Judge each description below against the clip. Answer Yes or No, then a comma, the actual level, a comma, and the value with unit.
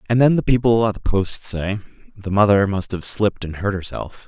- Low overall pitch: Yes, low, 105 Hz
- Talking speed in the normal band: No, fast, 225 wpm